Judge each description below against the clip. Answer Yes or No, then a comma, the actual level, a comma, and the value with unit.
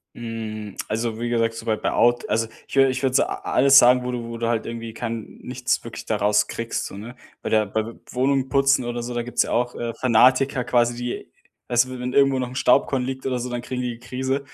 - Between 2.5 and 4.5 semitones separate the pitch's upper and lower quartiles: No, narrow, 1.9 semitones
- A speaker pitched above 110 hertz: Yes, low, 120 Hz